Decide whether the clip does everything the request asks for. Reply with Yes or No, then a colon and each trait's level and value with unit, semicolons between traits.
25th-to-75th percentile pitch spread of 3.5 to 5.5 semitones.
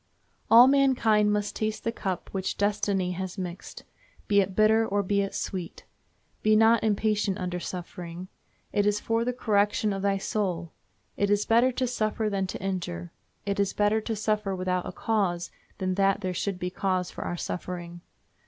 No: narrow, 2.6 semitones